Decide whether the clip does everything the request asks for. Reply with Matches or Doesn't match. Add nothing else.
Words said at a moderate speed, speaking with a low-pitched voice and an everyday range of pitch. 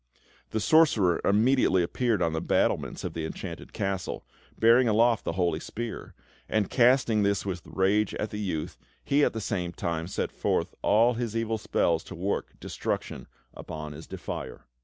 Matches